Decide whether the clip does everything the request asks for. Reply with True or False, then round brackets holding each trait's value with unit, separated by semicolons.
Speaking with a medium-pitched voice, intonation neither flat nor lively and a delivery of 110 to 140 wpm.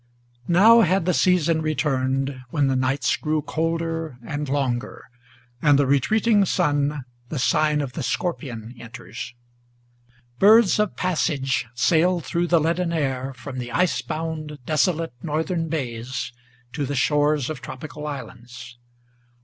True (150 Hz; 3.9 semitones; 135 wpm)